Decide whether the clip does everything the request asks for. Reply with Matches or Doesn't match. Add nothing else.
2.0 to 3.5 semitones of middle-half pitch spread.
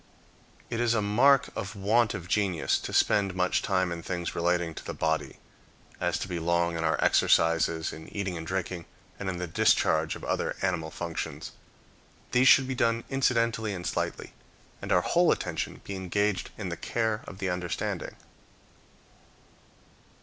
Doesn't match